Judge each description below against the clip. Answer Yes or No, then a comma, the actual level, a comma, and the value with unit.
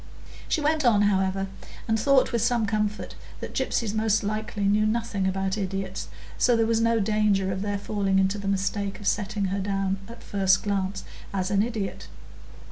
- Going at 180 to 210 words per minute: Yes, average, 185 wpm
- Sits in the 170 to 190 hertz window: No, high, 205 Hz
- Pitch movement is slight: Yes, narrow, 2.1 semitones